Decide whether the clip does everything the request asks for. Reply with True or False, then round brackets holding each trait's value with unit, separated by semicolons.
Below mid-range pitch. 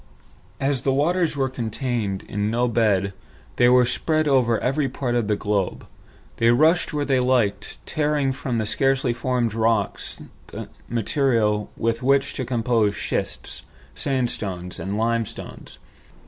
True (120 Hz)